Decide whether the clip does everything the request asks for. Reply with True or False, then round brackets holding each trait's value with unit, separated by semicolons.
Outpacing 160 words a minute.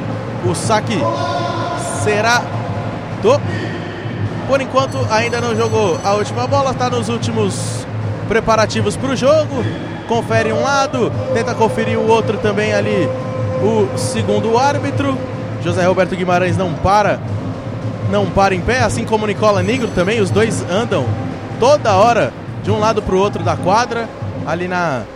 False (145 wpm)